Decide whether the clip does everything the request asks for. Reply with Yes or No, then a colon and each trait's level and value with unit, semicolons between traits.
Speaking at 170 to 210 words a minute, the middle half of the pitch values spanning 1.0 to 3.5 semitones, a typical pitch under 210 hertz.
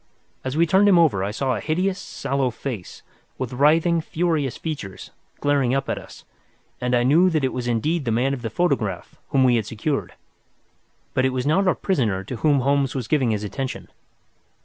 No: average, 195 wpm; average, 4.5 semitones; low, 135 Hz